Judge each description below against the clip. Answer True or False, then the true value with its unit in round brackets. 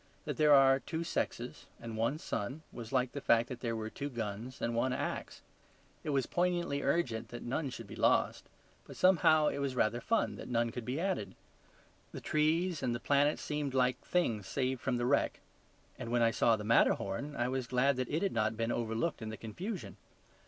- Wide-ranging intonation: False (4.3 semitones)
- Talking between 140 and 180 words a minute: False (205 wpm)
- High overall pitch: False (130 Hz)